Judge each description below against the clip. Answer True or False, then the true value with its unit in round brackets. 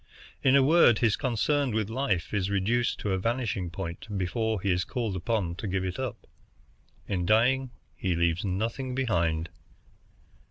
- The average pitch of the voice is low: True (105 Hz)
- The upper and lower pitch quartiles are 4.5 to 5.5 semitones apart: True (4.8 semitones)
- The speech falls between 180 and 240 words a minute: False (160 wpm)